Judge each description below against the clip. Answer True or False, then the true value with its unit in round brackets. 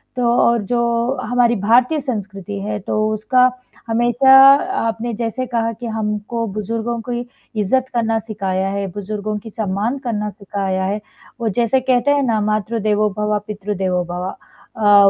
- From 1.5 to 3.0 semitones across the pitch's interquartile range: True (2.6 semitones)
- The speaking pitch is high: True (215 Hz)